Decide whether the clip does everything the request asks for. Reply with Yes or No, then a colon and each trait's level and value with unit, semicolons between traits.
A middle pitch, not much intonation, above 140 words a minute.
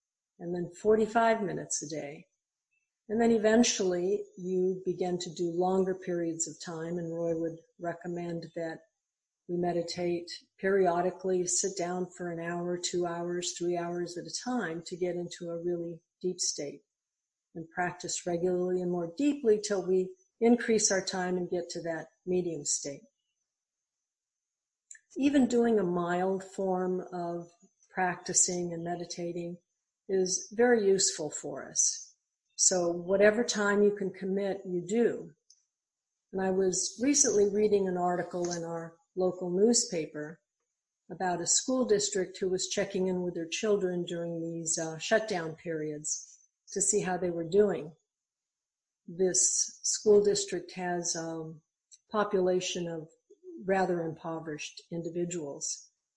No: medium, 180 Hz; narrow, 2.3 semitones; slow, 135 wpm